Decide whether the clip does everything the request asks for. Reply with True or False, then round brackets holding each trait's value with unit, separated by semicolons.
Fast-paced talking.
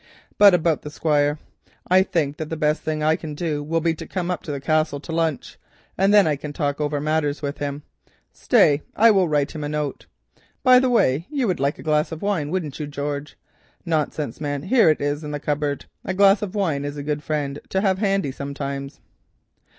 True (220 wpm)